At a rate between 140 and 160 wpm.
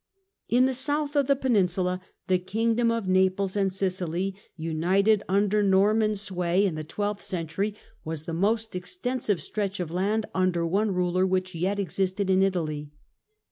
No: average, 170 wpm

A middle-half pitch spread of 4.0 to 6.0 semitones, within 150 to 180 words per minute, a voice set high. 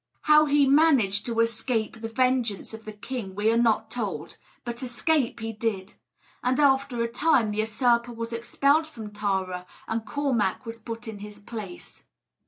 No: average, 3.2 semitones; average, 170 wpm; high, 230 Hz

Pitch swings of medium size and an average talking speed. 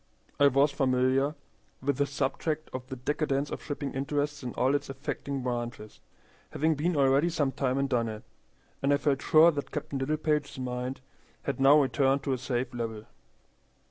No: narrow, 1.9 semitones; average, 170 wpm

